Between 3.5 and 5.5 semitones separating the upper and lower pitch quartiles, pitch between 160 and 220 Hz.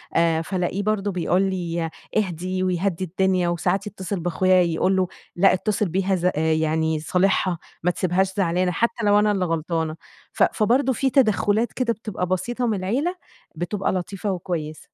No: average, 2.9 semitones; medium, 185 Hz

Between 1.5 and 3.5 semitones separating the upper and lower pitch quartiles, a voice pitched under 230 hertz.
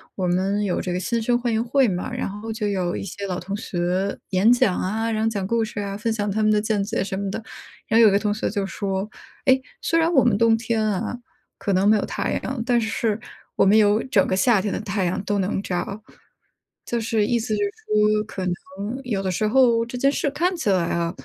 Yes: average, 2.9 semitones; high, 210 Hz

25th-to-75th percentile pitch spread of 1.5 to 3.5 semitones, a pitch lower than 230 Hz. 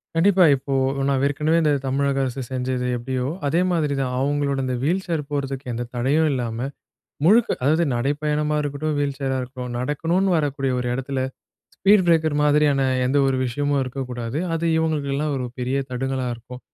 Yes: average, 2.7 semitones; medium, 140 Hz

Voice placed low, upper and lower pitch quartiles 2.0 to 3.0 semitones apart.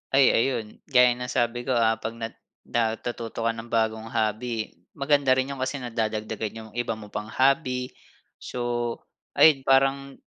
Yes: low, 120 Hz; average, 2.7 semitones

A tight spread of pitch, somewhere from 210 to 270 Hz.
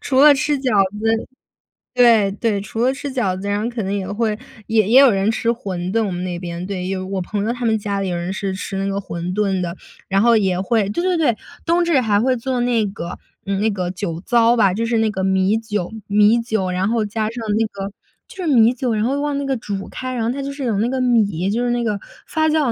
No: average, 3.7 semitones; high, 220 Hz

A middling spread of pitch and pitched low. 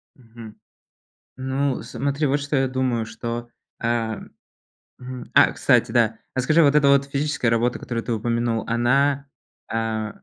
Yes: average, 3.2 semitones; low, 125 Hz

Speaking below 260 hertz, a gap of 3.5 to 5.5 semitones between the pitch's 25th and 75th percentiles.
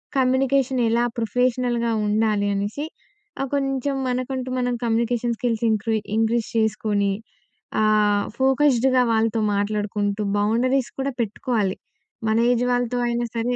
No: high, 235 Hz; average, 2.9 semitones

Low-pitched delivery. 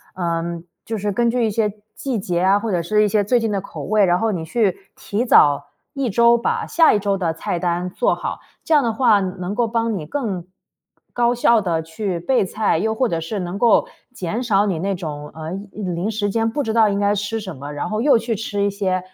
No: high, 205 Hz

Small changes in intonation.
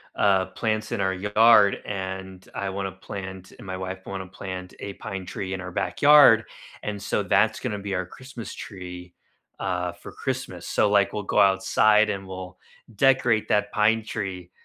Yes: narrow, 2.0 semitones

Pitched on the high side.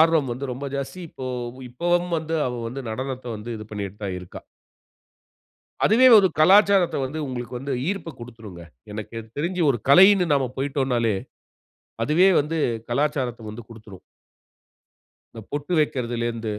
No: low, 135 Hz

